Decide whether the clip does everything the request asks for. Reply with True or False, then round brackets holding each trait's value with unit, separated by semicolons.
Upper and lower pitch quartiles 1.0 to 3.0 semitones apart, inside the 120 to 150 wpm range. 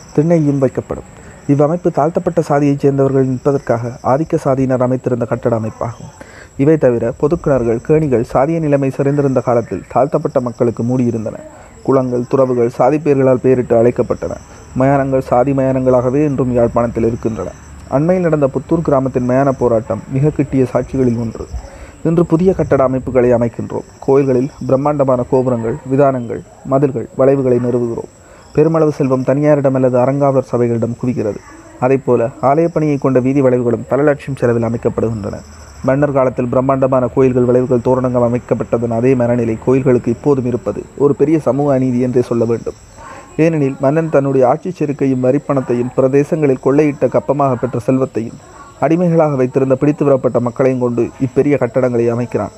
True (2.6 semitones; 125 wpm)